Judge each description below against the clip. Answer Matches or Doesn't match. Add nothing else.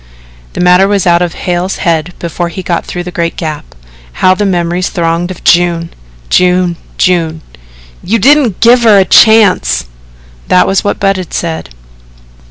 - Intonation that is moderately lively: Doesn't match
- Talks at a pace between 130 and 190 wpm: Matches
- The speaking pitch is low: Doesn't match